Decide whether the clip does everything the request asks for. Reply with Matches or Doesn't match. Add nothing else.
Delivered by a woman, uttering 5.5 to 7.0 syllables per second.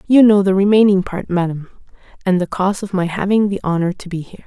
Matches